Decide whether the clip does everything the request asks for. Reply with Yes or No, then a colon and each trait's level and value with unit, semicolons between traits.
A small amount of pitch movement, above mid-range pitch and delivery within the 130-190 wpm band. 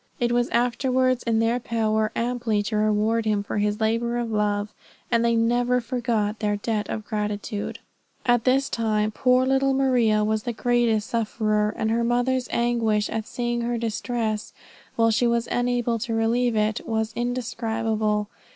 Yes: narrow, 2.0 semitones; high, 230 Hz; average, 160 wpm